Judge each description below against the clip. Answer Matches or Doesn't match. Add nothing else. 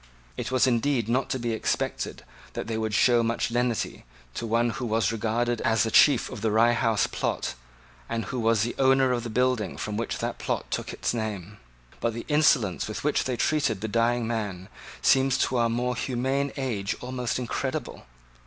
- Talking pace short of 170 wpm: Doesn't match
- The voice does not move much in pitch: Matches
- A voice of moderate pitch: Doesn't match